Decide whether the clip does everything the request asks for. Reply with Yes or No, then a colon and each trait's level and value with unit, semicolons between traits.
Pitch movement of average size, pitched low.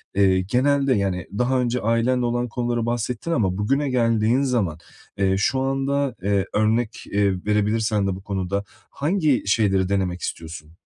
Yes: average, 4.3 semitones; low, 115 Hz